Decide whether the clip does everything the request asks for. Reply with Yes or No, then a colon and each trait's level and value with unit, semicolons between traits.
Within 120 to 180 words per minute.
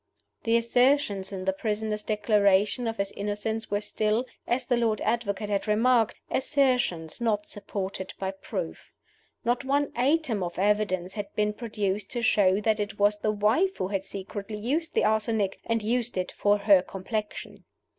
Yes: average, 165 wpm